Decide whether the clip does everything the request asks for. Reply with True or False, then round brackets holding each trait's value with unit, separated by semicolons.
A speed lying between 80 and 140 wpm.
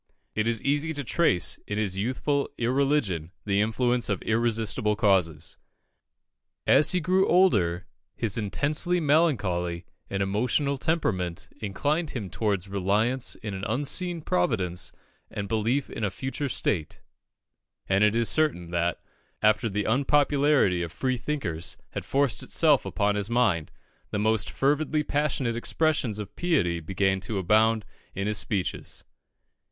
True (135 wpm)